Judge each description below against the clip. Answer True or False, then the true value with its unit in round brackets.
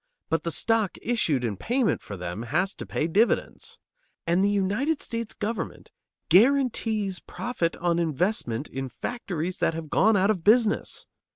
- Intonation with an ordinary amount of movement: False (5.7 semitones)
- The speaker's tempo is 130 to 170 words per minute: True (155 wpm)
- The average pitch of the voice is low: False (190 Hz)